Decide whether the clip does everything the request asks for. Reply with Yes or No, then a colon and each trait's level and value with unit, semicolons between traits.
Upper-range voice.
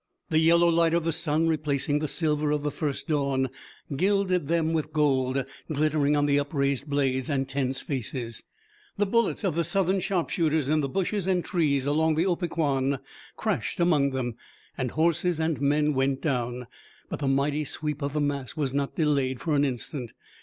No: medium, 150 Hz